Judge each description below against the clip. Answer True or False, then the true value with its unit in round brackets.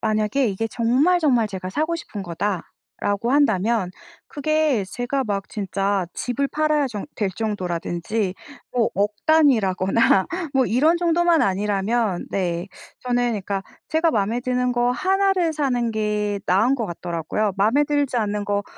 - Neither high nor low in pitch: False (225 Hz)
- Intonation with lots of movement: True (5.8 semitones)